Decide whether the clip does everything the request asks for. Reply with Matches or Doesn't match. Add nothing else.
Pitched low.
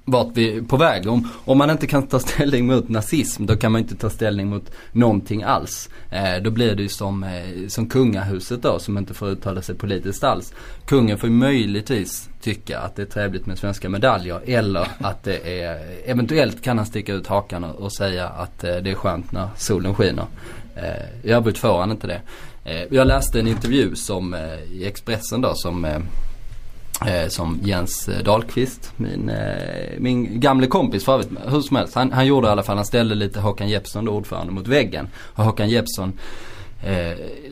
Matches